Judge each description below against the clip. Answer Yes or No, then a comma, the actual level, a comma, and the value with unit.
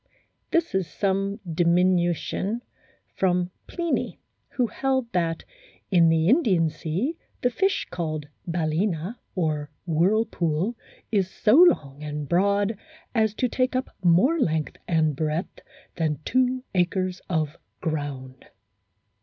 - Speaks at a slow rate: Yes, slow, 115 wpm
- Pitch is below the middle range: No, medium, 180 Hz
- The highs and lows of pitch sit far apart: Yes, wide, 5.8 semitones